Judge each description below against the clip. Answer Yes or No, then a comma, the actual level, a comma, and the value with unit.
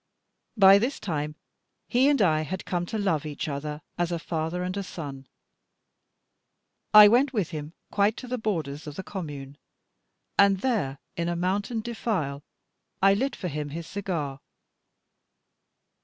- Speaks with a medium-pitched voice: Yes, medium, 175 Hz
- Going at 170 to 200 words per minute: No, average, 155 wpm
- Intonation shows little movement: No, average, 5.2 semitones